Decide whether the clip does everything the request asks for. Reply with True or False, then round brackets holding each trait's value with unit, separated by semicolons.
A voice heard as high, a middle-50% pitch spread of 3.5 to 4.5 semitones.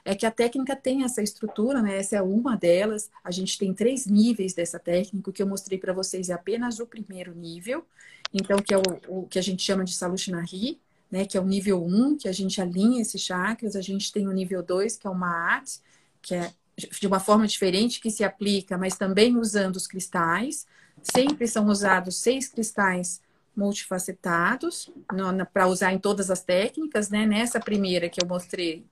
False (195 Hz; 2.8 semitones)